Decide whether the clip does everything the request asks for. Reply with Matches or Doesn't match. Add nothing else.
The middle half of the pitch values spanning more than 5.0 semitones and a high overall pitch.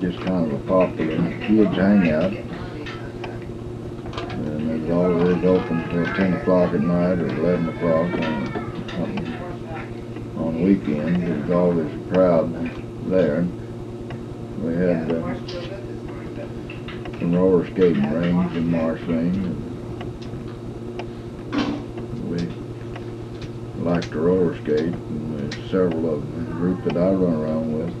Doesn't match